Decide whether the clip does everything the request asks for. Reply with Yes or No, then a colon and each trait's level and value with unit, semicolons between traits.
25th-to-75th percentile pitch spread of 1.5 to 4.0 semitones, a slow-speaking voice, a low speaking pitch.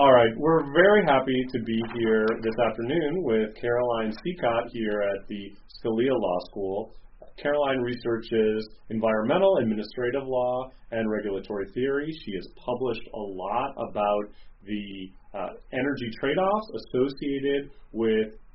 Yes: average, 3.5 semitones; slow, 130 wpm; low, 115 Hz